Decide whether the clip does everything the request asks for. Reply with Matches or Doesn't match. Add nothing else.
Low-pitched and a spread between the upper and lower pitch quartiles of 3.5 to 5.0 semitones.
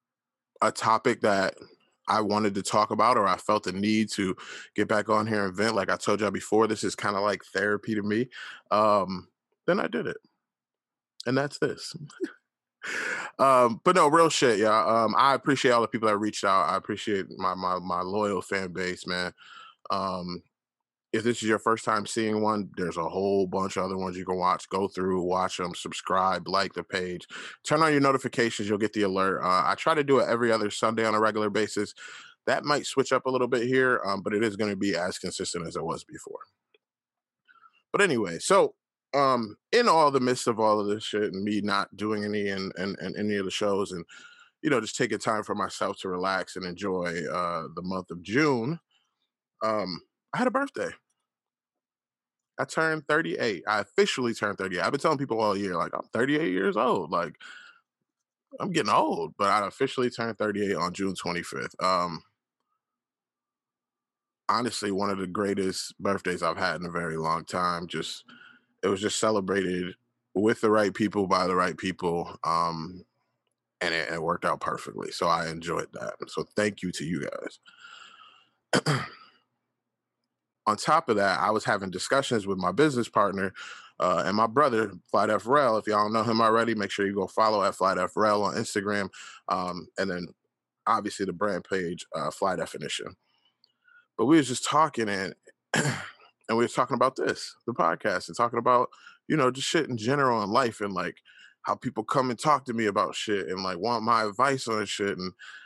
Matches